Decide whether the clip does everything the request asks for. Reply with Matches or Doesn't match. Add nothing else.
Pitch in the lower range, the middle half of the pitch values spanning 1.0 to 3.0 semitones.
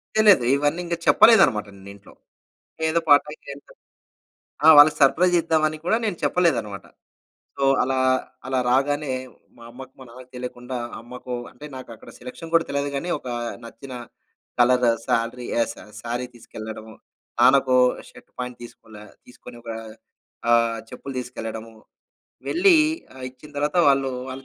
Doesn't match